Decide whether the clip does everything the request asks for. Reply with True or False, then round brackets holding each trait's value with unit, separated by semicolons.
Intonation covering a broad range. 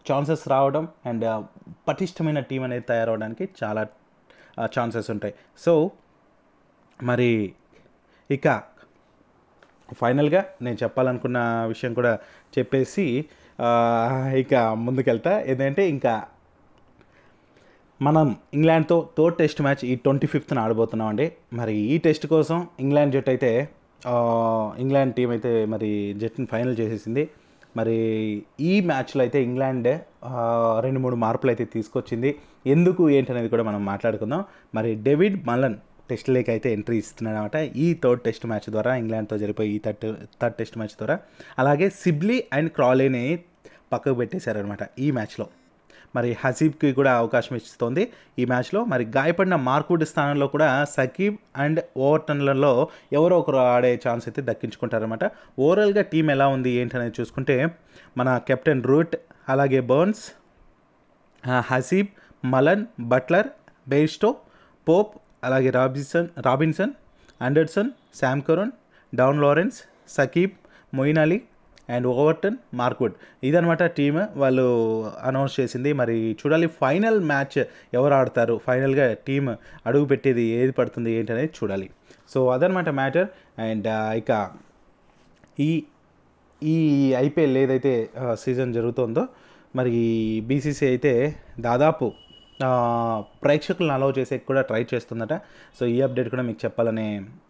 False (4.7 semitones)